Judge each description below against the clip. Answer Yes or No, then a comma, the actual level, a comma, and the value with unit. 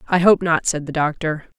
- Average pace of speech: No, fast, 225 wpm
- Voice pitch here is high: No, medium, 165 Hz